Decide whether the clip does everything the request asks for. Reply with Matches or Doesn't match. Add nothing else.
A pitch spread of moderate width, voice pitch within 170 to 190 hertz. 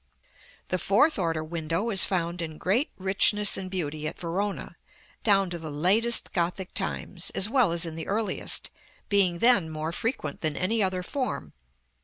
Matches